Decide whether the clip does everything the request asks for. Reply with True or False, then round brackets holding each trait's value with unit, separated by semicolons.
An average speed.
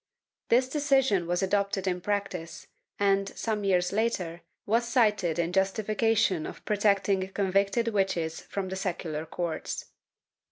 False (130 wpm)